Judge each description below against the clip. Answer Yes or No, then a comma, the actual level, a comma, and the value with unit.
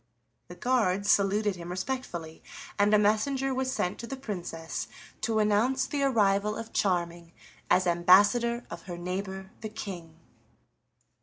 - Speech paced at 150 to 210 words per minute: No, average, 140 wpm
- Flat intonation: No, average, 4.6 semitones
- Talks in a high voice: Yes, high, 205 Hz